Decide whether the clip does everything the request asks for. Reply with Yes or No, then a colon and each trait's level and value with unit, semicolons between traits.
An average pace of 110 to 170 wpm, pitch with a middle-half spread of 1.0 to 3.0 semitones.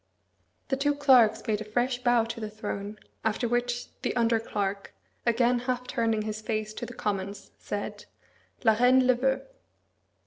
Yes: average, 165 wpm; narrow, 2.5 semitones